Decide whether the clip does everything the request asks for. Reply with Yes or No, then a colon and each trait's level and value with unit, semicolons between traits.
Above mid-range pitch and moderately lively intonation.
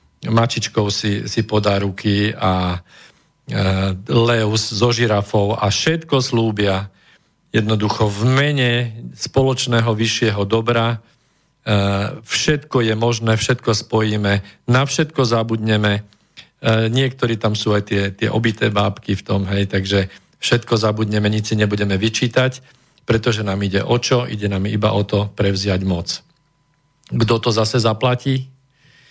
No: low, 110 Hz; average, 3.2 semitones